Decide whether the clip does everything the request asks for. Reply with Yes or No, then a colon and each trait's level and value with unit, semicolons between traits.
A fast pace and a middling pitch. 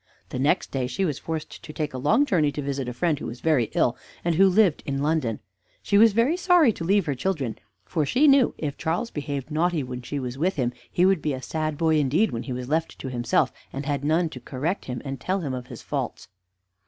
Yes: fast, 245 wpm; medium, 150 Hz